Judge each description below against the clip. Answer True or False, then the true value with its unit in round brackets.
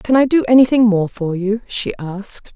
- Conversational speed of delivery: False (210 wpm)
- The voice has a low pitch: False (215 Hz)